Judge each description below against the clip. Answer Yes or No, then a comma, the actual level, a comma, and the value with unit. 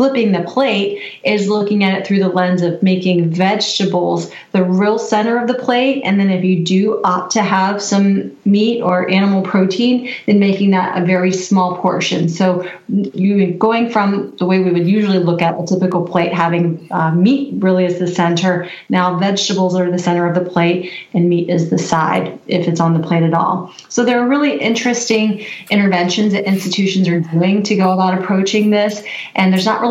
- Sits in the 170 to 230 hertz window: Yes, high, 190 Hz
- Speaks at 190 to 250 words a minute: Yes, average, 200 wpm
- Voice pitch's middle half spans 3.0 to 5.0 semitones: No, narrow, 2.5 semitones